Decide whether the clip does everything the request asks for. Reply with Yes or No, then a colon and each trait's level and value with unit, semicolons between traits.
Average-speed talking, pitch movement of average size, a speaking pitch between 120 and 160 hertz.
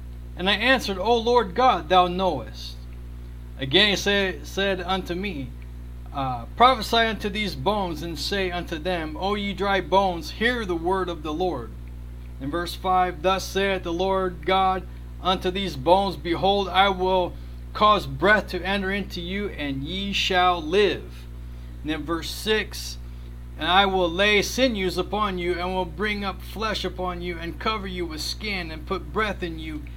No: average, 170 wpm; average, 4.1 semitones; medium, 185 Hz